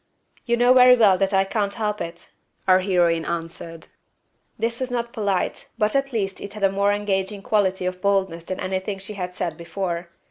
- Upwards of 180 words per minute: Yes, average, 190 wpm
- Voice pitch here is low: No, high, 195 Hz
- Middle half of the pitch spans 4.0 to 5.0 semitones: No, average, 2.7 semitones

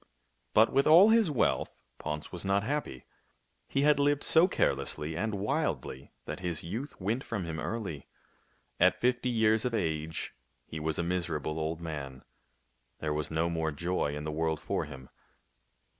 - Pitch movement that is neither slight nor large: No, wide, 7.4 semitones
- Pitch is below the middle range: Yes, very low, 85 Hz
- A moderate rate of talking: Yes, average, 165 wpm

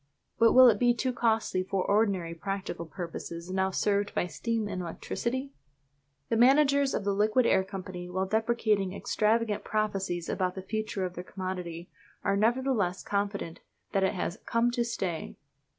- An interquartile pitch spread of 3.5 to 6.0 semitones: Yes, average, 3.8 semitones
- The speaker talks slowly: No, average, 160 wpm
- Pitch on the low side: No, high, 200 Hz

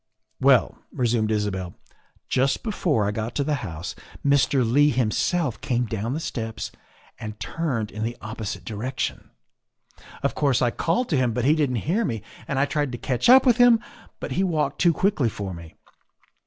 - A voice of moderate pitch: No, low, 125 Hz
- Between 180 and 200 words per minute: Yes, average, 185 wpm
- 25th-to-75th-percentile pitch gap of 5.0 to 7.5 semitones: Yes, average, 5.3 semitones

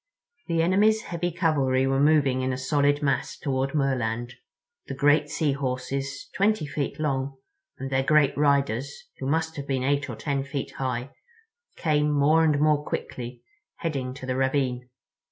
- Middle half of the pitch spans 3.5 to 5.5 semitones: No, narrow, 2.4 semitones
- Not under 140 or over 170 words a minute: Yes, average, 155 wpm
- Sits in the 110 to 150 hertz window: Yes, medium, 140 Hz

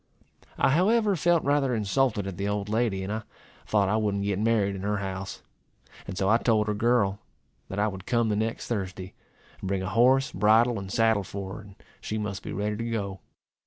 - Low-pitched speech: Yes, low, 105 Hz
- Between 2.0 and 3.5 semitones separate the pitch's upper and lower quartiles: Yes, average, 2.9 semitones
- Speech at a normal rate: No, fast, 210 wpm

